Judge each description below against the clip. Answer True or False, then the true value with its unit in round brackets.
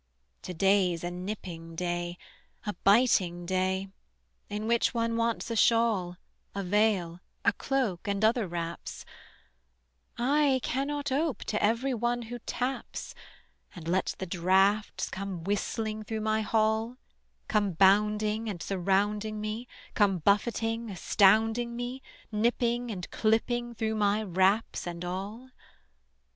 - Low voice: False (210 Hz)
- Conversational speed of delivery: False (125 wpm)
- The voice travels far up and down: False (3.5 semitones)